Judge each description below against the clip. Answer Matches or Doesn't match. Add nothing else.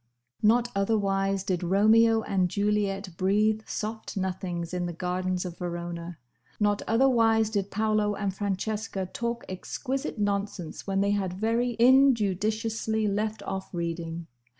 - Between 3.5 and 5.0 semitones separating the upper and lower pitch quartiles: Doesn't match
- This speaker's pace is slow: Matches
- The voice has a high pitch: Matches